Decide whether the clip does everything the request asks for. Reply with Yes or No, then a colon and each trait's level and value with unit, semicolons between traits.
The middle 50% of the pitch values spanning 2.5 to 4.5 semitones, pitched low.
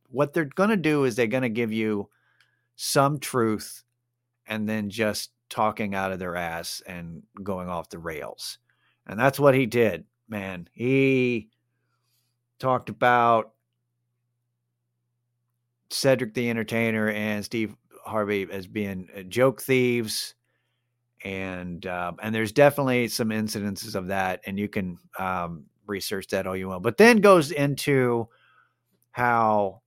Yes: average, 3.3 semitones; low, 115 Hz